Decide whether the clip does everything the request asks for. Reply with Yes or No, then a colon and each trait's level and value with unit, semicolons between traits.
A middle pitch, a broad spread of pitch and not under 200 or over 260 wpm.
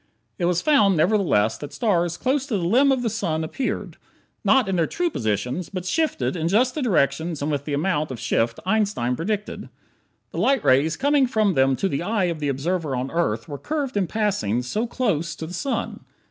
Yes: medium, 175 Hz; wide, 7.3 semitones; fast, 205 wpm